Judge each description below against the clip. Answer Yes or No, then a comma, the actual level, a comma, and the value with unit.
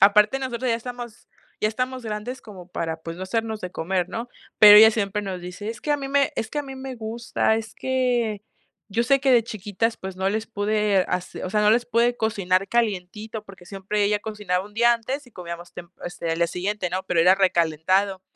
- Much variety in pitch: No, average, 3.9 semitones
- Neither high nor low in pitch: No, high, 210 Hz